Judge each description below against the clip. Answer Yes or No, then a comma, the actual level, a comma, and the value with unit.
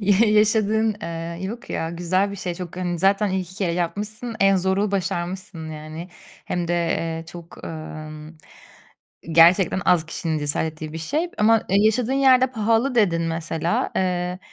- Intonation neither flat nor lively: Yes, average, 4.1 semitones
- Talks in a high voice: No, medium, 180 Hz